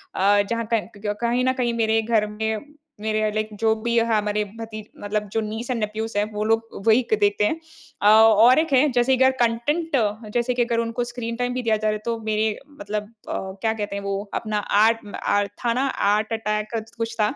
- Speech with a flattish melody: Yes, narrow, 1.9 semitones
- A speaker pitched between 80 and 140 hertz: No, high, 220 Hz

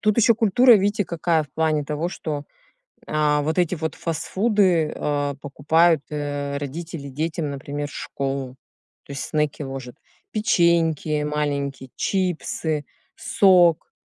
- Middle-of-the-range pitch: Yes, medium, 155 Hz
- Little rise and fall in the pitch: No, average, 3.2 semitones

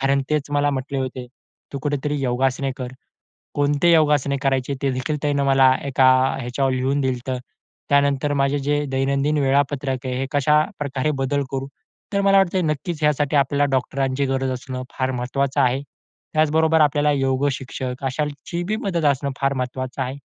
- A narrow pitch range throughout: Yes, narrow, 1.9 semitones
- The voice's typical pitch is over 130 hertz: Yes, medium, 140 Hz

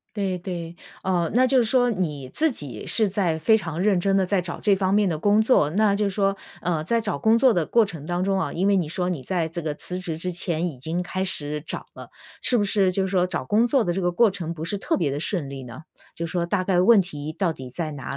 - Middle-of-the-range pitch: Yes, medium, 180 Hz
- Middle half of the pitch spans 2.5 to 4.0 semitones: Yes, average, 3.7 semitones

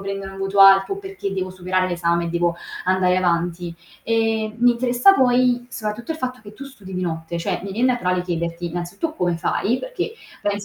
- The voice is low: No, high, 195 Hz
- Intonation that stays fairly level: No, wide, 5.4 semitones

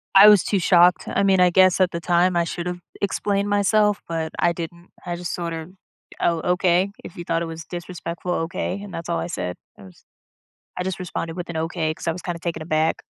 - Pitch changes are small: Yes, narrow, 1.9 semitones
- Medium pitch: Yes, medium, 175 Hz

